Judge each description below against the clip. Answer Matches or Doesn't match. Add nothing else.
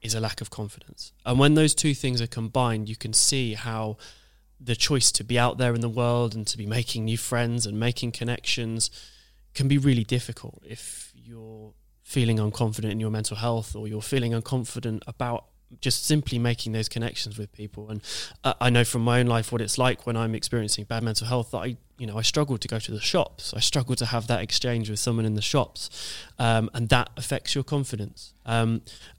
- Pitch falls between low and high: Doesn't match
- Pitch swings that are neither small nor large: Doesn't match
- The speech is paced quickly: Matches